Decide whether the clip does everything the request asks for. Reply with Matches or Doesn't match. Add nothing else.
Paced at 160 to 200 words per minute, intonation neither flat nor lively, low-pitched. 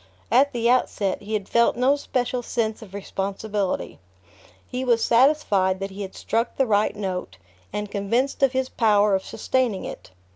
Doesn't match